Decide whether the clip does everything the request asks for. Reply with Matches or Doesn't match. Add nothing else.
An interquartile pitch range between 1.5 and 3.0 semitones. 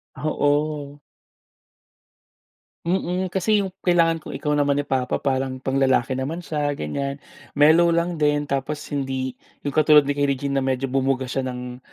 Matches